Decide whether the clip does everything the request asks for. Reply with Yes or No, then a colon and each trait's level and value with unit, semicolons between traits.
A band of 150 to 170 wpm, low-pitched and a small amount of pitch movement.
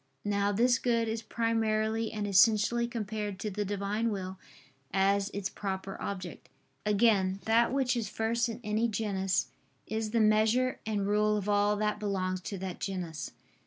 No: average, 160 wpm; high, 210 Hz; narrow, 2.2 semitones